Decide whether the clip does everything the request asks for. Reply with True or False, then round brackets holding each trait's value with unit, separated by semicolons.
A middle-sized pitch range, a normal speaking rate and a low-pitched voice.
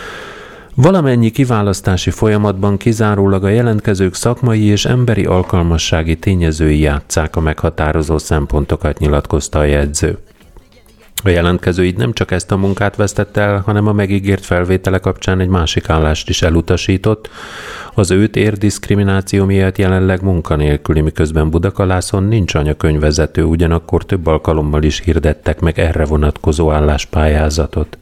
True (4.3 semitones; 125 wpm; 90 Hz)